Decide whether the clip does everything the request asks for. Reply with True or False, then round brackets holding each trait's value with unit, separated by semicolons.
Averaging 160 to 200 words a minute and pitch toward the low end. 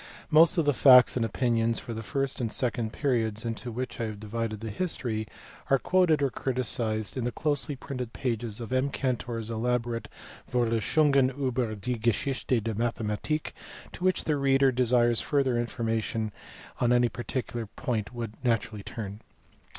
True (165 wpm; 120 Hz)